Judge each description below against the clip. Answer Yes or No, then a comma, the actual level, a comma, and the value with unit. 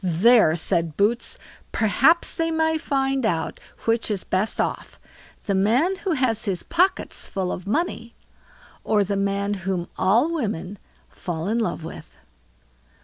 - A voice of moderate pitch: No, high, 215 Hz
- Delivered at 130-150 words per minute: Yes, average, 145 wpm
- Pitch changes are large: Yes, wide, 6.1 semitones